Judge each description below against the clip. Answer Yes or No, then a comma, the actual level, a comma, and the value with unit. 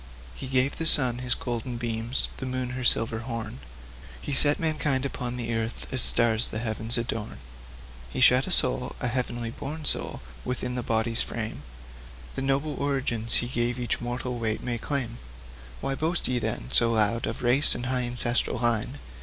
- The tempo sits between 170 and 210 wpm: Yes, average, 180 wpm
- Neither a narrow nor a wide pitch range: No, narrow, 2.0 semitones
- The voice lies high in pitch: No, low, 120 Hz